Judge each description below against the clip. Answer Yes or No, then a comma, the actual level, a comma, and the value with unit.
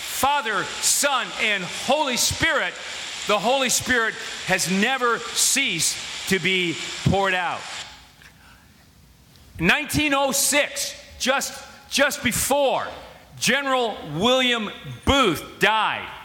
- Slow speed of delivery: Yes, slow, 85 wpm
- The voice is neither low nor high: No, high, 245 Hz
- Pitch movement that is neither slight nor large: No, wide, 5.8 semitones